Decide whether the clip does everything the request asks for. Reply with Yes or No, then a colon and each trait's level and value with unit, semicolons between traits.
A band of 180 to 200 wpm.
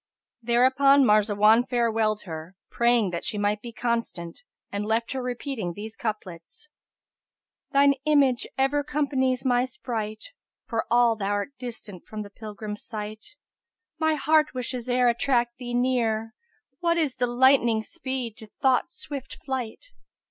No: average, 145 wpm